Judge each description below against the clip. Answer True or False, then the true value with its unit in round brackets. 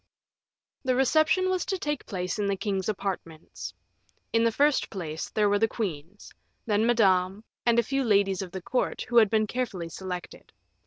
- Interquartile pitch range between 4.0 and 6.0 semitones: True (4.3 semitones)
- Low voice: False (210 Hz)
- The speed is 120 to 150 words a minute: False (175 wpm)